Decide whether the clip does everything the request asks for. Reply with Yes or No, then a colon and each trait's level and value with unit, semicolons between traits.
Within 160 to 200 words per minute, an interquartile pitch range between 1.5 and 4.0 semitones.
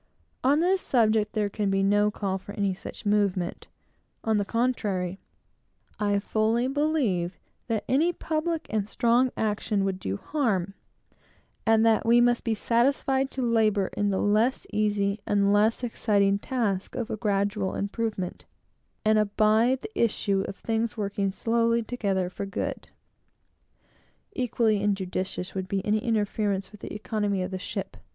No: average, 145 wpm; average, 2.8 semitones